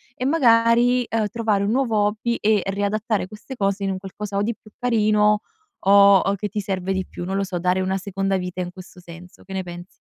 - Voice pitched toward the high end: Yes, high, 200 Hz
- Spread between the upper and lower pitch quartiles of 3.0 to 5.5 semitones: No, narrow, 2.5 semitones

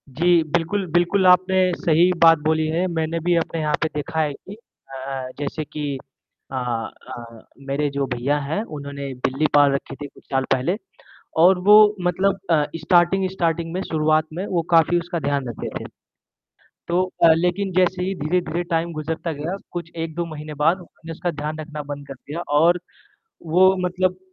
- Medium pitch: Yes, medium, 165 Hz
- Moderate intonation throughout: Yes, average, 3.3 semitones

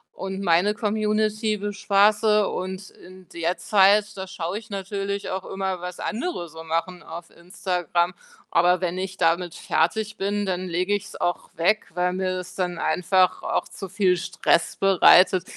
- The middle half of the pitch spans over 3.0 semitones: No, narrow, 2.4 semitones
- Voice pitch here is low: No, medium, 185 Hz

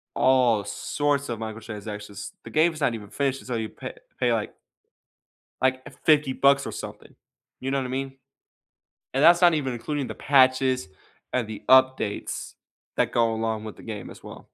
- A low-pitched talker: Yes, low, 130 Hz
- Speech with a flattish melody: No, average, 3.7 semitones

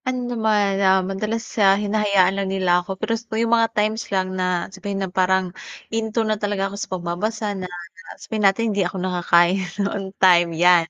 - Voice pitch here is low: No, high, 195 Hz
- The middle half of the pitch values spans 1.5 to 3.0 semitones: Yes, average, 2.7 semitones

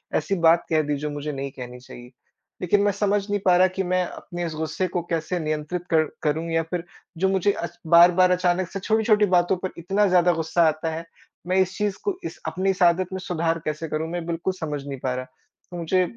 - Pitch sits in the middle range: Yes, medium, 175 Hz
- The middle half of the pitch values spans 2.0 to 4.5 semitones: Yes, average, 2.8 semitones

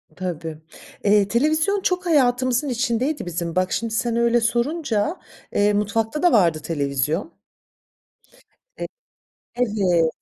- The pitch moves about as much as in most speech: No, wide, 6.0 semitones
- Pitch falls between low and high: No, high, 225 Hz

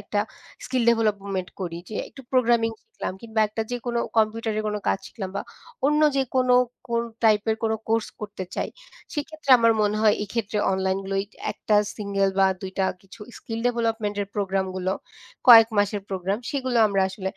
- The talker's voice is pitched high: Yes, high, 215 Hz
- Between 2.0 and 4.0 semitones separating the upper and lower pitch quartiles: Yes, average, 2.9 semitones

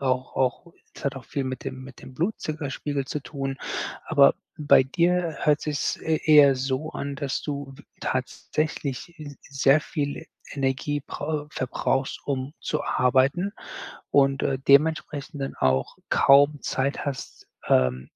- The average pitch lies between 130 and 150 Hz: Yes, medium, 140 Hz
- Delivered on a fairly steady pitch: Yes, narrow, 2.1 semitones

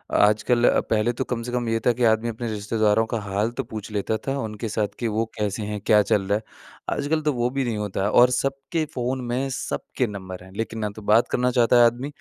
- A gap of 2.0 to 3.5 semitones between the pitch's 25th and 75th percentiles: Yes, average, 2.8 semitones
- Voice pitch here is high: No, low, 115 Hz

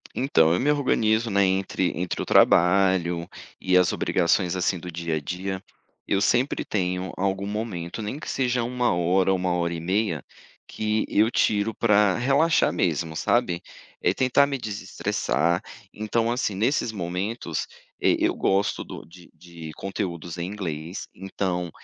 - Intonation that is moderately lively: Yes, average, 3.9 semitones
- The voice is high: No, very low, 95 Hz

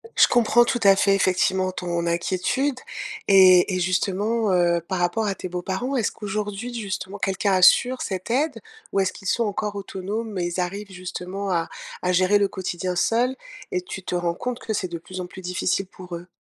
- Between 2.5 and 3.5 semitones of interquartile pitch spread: Yes, average, 2.8 semitones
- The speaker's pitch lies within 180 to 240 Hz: Yes, high, 190 Hz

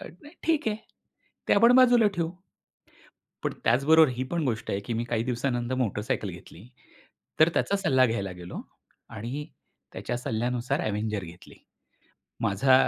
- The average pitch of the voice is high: No, low, 120 Hz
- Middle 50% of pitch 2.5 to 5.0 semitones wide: No, wide, 5.4 semitones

